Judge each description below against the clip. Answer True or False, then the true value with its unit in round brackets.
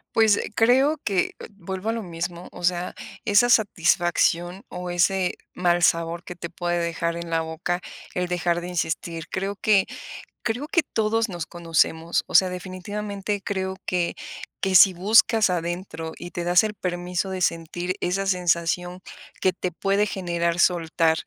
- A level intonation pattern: True (2.3 semitones)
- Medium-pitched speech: True (180 Hz)